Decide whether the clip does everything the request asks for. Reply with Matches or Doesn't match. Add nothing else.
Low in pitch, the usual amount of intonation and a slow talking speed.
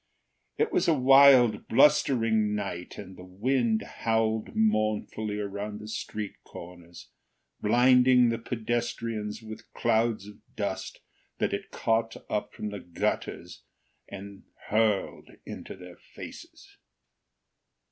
Doesn't match